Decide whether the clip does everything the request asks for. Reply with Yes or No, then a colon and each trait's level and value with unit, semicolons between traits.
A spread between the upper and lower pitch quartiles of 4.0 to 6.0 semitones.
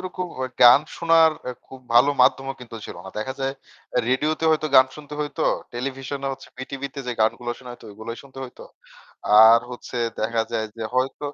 No: average, 2.7 semitones